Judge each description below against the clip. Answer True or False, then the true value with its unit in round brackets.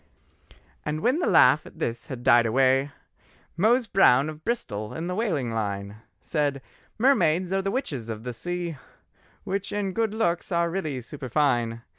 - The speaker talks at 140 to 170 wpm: True (160 wpm)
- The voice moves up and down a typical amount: False (7.8 semitones)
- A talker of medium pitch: True (155 Hz)